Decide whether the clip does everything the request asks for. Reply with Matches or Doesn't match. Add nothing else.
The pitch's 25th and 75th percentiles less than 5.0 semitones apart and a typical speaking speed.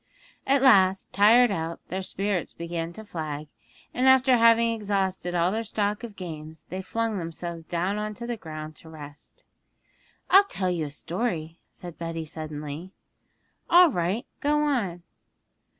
Doesn't match